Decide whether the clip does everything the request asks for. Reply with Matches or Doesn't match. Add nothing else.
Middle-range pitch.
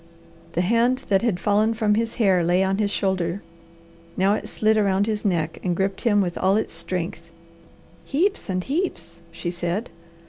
Doesn't match